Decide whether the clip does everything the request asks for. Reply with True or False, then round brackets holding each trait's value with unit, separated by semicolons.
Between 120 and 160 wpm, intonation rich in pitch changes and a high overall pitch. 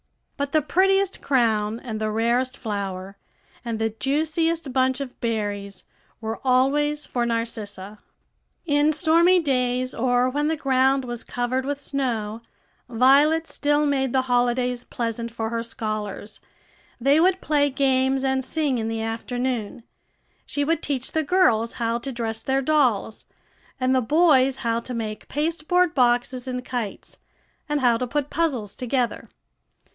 False (145 wpm; 3.9 semitones; 255 Hz)